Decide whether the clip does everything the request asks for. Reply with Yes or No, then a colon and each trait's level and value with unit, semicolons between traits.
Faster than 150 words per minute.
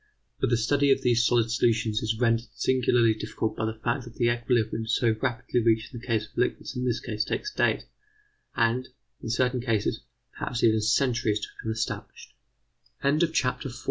Yes: average, 175 wpm